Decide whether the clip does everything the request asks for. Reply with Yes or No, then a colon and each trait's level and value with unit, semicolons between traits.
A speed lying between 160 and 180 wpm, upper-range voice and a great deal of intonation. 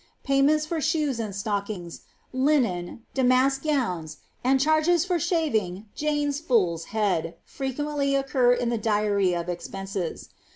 No: slow, 135 wpm; very high, 250 Hz; wide, 6.8 semitones